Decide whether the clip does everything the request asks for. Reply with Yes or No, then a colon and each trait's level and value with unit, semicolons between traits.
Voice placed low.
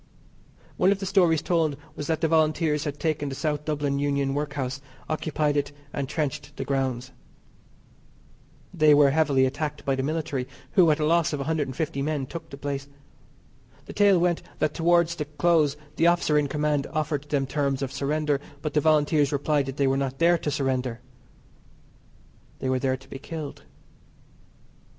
No: medium, 150 Hz